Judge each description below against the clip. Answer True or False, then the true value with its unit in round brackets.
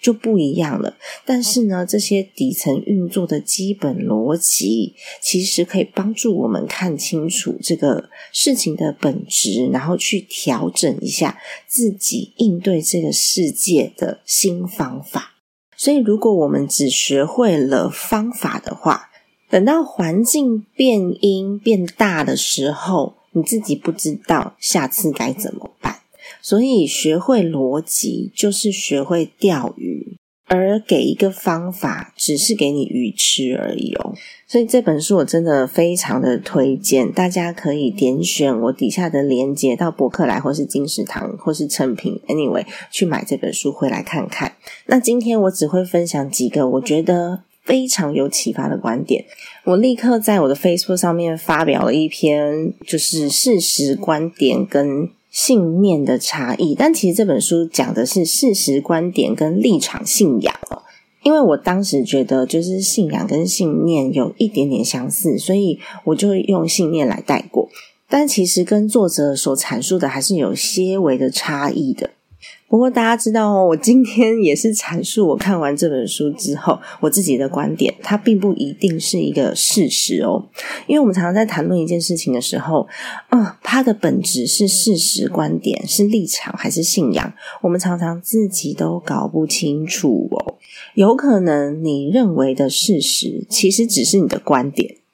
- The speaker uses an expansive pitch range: True (6.1 semitones)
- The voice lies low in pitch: False (185 Hz)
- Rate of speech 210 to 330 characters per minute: True (250 characters per minute)